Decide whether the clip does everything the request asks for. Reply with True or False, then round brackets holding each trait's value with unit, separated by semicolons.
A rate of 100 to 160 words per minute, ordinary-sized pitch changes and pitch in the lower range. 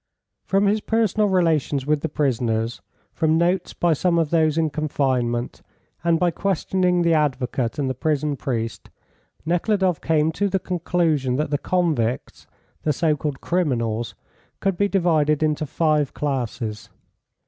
False (145 wpm; 4.4 semitones; 155 Hz)